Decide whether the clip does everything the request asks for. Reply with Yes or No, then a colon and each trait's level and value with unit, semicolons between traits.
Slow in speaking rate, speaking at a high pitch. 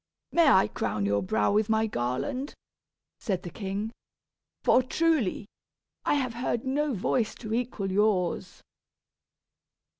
Yes: slow, 125 wpm; high, 220 Hz